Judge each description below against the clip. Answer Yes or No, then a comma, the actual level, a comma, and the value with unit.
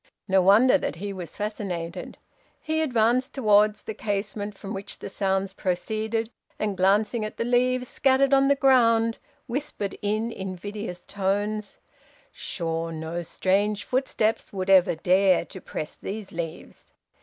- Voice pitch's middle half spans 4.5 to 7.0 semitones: No, average, 3.3 semitones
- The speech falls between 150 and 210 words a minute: No, average, 140 wpm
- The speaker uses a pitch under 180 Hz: No, high, 205 Hz